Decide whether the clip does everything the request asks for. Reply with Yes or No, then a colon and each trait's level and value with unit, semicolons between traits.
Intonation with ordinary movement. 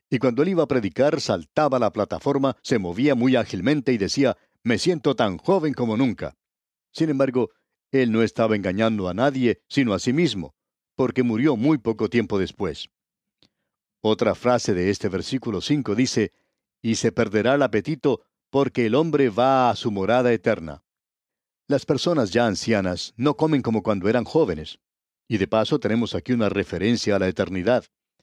Yes: average, 4.0 semitones